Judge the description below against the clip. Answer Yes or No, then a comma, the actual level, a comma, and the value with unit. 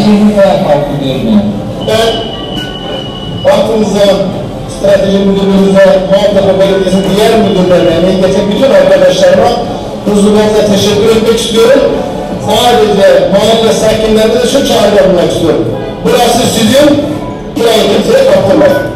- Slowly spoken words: Yes, slow, 90 wpm